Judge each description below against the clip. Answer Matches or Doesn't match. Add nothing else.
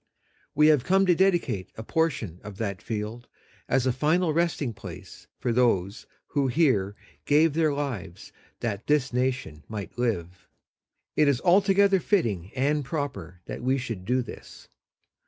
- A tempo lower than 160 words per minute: Matches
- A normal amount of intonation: Doesn't match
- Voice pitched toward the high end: Doesn't match